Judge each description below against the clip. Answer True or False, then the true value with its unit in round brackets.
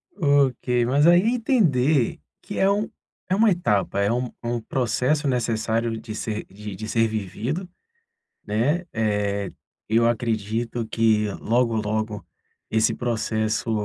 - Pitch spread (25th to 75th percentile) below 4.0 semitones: False (4.3 semitones)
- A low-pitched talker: True (115 Hz)